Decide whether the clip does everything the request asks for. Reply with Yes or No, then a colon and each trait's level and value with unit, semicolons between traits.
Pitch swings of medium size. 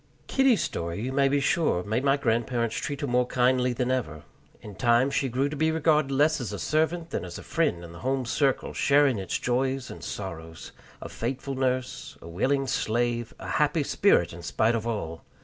Yes: average, 3.9 semitones